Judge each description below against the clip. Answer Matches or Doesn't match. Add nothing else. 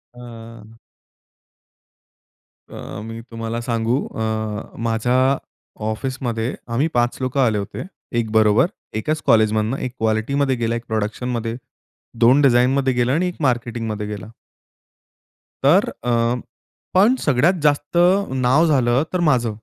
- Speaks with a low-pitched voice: Matches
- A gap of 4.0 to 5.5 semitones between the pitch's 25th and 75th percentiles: Doesn't match